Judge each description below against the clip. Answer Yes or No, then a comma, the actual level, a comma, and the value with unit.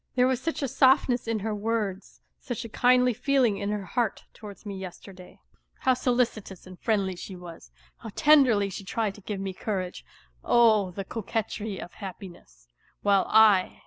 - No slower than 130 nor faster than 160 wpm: No, average, 175 wpm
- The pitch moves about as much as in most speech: Yes, average, 3.9 semitones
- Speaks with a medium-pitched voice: No, high, 210 Hz